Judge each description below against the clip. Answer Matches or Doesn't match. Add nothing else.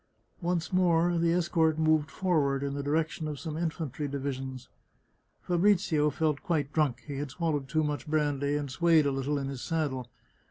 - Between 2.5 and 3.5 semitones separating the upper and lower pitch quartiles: Matches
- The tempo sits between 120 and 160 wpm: Doesn't match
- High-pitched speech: Doesn't match